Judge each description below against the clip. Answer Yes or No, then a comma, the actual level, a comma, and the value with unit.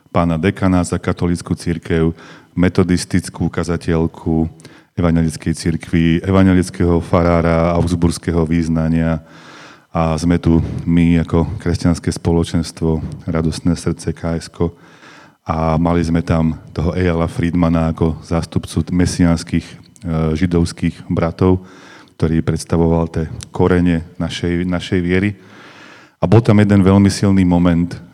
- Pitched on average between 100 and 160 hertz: No, very low, 85 Hz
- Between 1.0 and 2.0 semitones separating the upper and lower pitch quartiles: Yes, narrow, 1.4 semitones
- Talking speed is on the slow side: Yes, slow, 105 wpm